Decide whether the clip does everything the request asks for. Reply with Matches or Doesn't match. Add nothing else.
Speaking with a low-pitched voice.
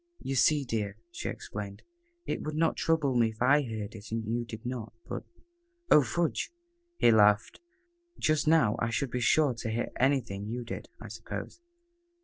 Matches